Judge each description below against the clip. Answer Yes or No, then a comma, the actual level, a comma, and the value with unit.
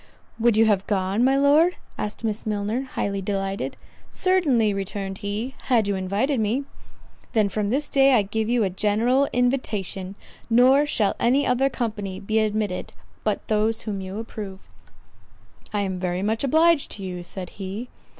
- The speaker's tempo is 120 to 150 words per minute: No, average, 160 wpm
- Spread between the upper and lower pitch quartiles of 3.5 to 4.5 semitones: Yes, average, 4.1 semitones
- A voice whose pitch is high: Yes, high, 215 Hz